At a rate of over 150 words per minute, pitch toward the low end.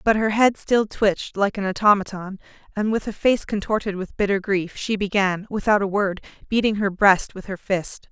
No: average, 200 wpm; high, 200 Hz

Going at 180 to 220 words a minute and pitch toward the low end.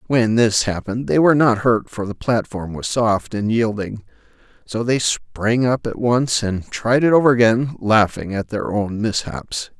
Yes: average, 185 wpm; low, 110 Hz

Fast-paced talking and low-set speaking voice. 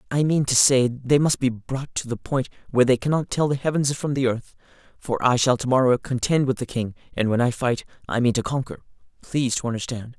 Yes: fast, 230 wpm; low, 130 Hz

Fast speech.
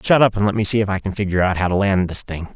Yes: fast, 375 wpm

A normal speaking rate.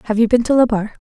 No: fast, 290 wpm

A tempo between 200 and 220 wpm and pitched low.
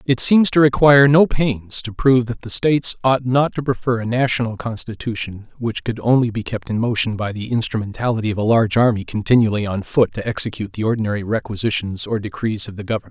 Yes: fast, 205 wpm; low, 115 Hz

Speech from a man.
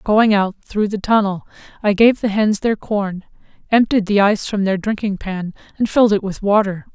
No: female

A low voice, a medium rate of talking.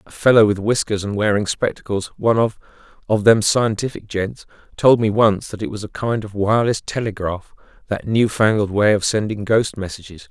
Yes: low, 105 Hz; average, 170 wpm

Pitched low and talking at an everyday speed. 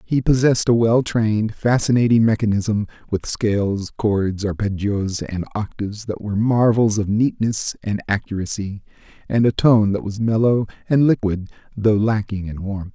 Yes: low, 105 Hz; average, 150 wpm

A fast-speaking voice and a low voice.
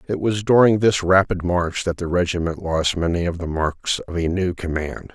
Yes: fast, 210 wpm; very low, 90 Hz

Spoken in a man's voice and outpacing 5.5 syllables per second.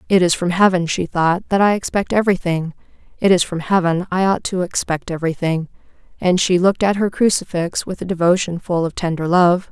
No: female; 5.7 syllables/s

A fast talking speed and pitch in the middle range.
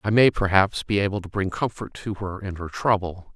No: fast, 230 wpm; very low, 95 Hz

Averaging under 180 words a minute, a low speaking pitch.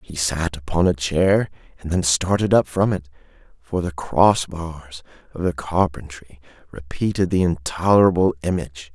Yes: average, 150 wpm; very low, 85 Hz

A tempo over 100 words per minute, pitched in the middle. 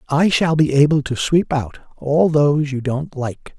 Yes: average, 200 wpm; medium, 145 Hz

